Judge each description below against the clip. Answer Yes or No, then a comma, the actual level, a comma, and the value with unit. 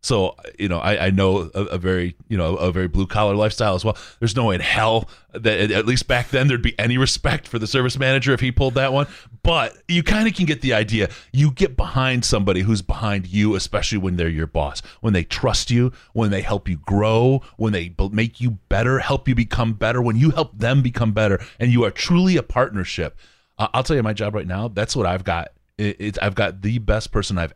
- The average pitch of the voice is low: Yes, low, 110 Hz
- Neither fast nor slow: No, fast, 235 wpm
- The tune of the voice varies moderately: Yes, average, 4.1 semitones